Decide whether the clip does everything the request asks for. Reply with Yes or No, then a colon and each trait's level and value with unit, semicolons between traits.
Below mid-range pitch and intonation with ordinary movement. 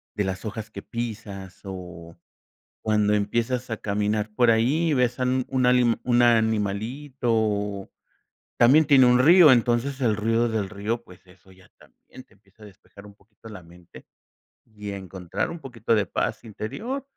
Yes: low, 110 Hz; average, 3.5 semitones